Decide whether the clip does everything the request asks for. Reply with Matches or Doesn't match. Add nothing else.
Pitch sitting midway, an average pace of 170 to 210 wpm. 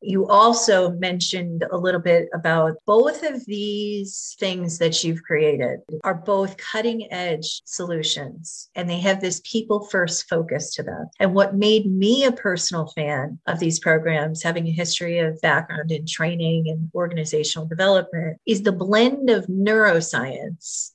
Doesn't match